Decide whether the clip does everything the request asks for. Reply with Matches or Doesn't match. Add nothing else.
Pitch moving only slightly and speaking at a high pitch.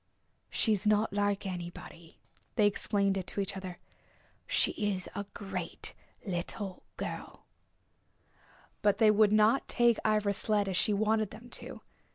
Matches